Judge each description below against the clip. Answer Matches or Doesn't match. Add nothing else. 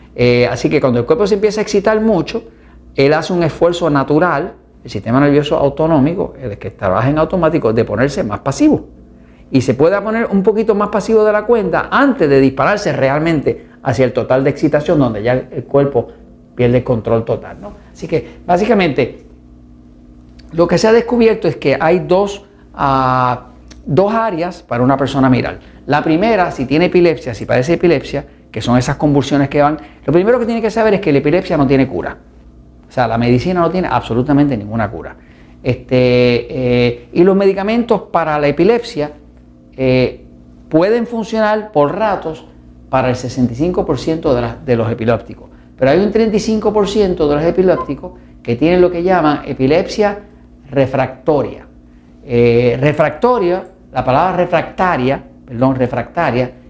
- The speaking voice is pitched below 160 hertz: Matches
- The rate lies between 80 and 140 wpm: Doesn't match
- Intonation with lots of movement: Matches